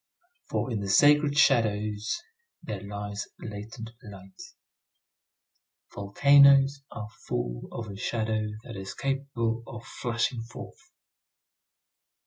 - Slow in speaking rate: Yes, slow, 105 wpm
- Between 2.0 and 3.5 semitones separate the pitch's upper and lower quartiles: No, average, 4.8 semitones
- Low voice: Yes, low, 115 Hz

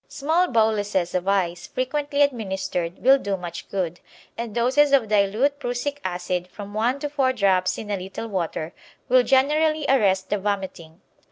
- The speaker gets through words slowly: No, average, 160 wpm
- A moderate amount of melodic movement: No, wide, 6.2 semitones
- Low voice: No, high, 210 Hz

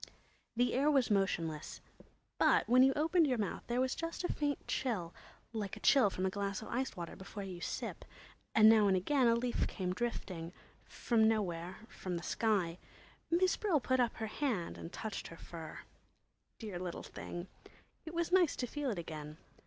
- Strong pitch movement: Yes, wide, 6.2 semitones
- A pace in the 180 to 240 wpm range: Yes, average, 185 wpm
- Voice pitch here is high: Yes, high, 220 Hz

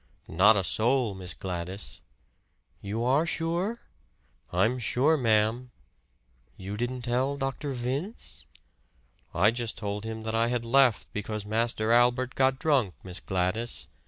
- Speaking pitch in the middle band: No, low, 115 Hz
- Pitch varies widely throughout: No, average, 3.8 semitones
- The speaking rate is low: Yes, slow, 130 wpm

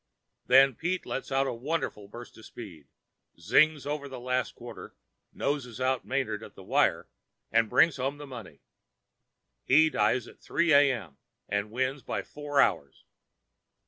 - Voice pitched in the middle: No, low, 130 Hz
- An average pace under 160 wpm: Yes, average, 150 wpm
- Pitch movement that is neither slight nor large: Yes, average, 4.1 semitones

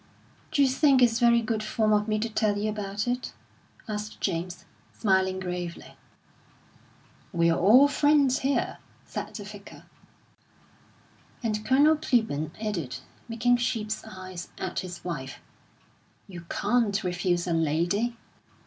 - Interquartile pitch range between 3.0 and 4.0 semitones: No, average, 4.9 semitones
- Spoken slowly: Yes, slow, 125 wpm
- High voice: Yes, high, 210 Hz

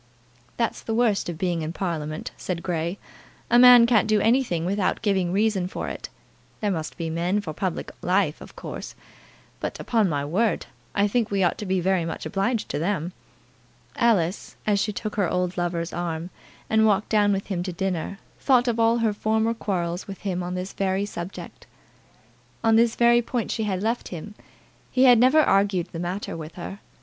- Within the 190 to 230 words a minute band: Yes, average, 195 wpm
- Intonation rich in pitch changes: No, average, 4.0 semitones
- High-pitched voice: Yes, high, 195 Hz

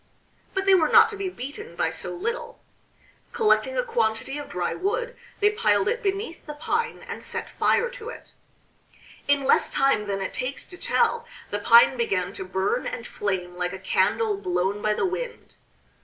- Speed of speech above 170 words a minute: Yes, average, 185 wpm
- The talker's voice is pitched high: Yes, very high, 375 Hz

